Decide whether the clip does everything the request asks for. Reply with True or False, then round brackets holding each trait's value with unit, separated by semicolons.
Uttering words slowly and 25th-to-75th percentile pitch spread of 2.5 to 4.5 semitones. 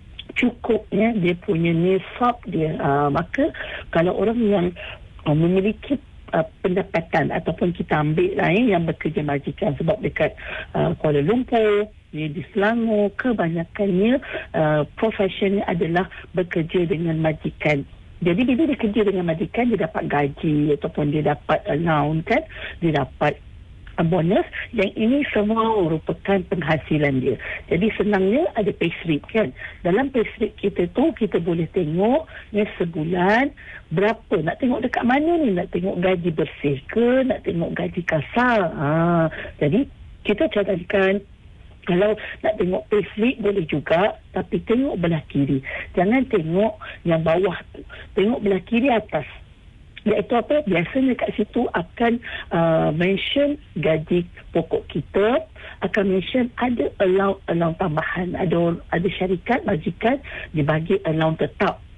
False (130 wpm; 5.1 semitones)